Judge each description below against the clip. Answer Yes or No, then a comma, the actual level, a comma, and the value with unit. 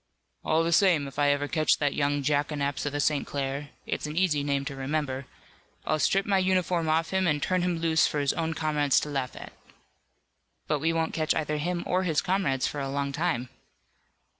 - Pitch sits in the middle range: Yes, medium, 150 Hz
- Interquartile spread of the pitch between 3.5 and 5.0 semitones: No, narrow, 2.6 semitones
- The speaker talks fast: Yes, fast, 210 wpm